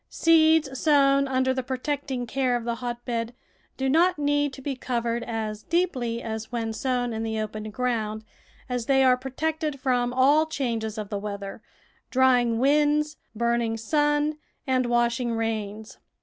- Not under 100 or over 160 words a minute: Yes, average, 155 wpm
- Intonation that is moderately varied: Yes, average, 3.4 semitones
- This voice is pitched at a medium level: No, very high, 250 Hz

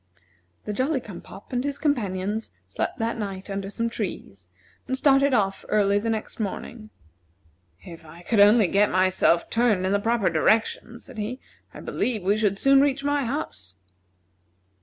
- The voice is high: Yes, high, 215 Hz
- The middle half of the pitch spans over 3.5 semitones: Yes, average, 4.1 semitones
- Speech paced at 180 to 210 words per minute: No, average, 165 wpm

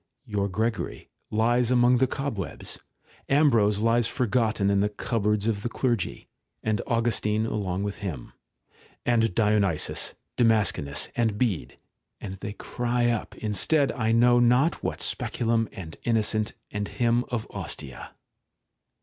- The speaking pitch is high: No, low, 110 Hz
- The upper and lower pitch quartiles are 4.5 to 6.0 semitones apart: No, average, 2.7 semitones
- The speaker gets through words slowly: Yes, slow, 125 wpm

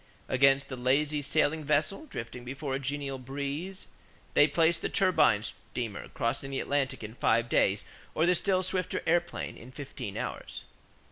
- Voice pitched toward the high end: No, medium, 140 Hz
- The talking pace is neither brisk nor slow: Yes, average, 155 wpm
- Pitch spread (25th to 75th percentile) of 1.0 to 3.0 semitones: No, average, 3.9 semitones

